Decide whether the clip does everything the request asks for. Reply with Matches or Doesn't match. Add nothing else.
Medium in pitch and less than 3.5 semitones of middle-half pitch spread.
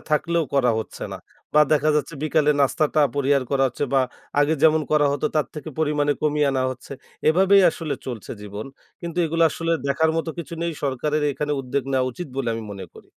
Matches